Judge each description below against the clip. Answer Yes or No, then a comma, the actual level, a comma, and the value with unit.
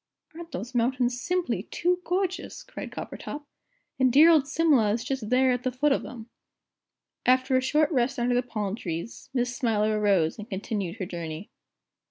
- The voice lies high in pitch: Yes, very high, 250 Hz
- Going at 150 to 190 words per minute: Yes, average, 175 wpm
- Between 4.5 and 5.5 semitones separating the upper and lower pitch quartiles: Yes, average, 5.2 semitones